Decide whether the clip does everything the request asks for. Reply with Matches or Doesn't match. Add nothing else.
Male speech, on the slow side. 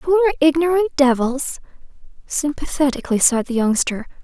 Doesn't match